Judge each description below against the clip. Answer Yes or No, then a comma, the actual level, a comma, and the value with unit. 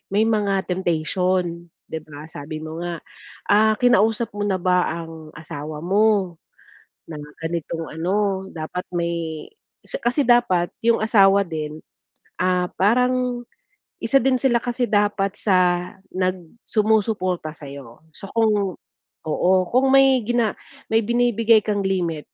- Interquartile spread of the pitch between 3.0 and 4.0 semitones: No, average, 4.7 semitones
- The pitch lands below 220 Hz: Yes, high, 190 Hz